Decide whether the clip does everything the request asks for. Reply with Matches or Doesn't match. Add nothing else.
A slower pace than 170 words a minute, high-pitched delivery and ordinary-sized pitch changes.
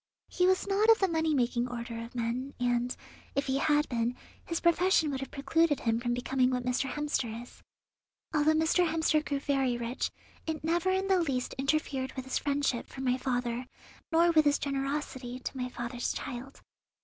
Doesn't match